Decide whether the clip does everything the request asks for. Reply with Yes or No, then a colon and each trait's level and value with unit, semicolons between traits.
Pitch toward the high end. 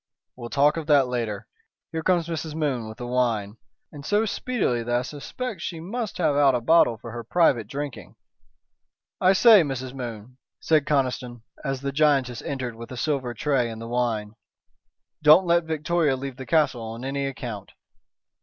No: low, 135 Hz